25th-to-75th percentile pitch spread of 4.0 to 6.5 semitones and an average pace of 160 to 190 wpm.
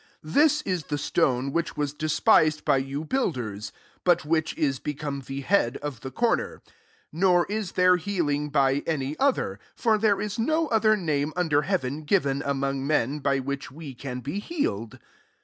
Yes: average, 5.0 semitones; average, 180 wpm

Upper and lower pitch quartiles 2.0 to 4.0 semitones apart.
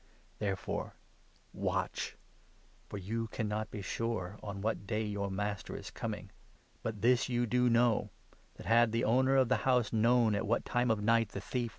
Yes: narrow, 2.6 semitones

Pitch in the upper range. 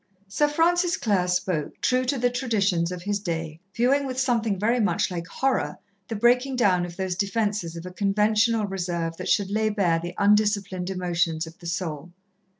Yes: high, 200 Hz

